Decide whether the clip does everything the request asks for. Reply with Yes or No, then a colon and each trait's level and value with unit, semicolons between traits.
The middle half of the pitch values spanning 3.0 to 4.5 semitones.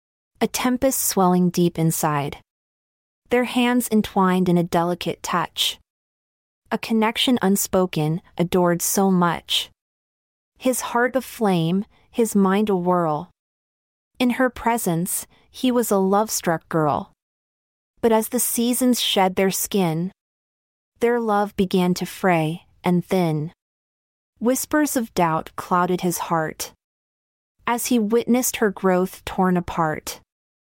No: average, 5.1 semitones